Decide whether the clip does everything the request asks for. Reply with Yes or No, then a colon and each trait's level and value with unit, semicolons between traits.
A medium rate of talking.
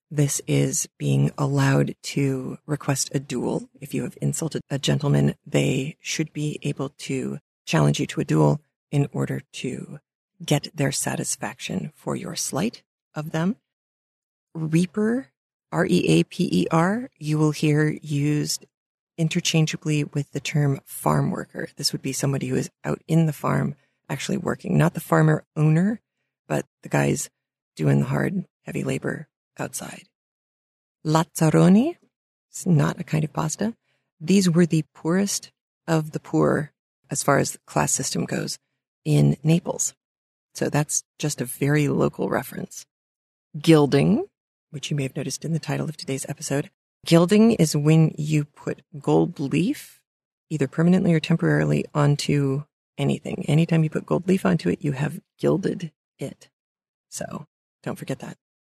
Yes: average, 150 wpm